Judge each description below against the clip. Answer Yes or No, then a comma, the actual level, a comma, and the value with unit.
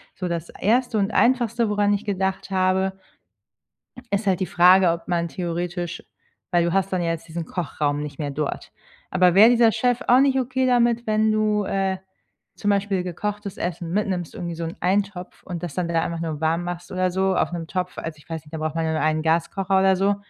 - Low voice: No, medium, 185 Hz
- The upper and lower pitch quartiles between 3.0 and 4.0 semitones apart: Yes, average, 3.3 semitones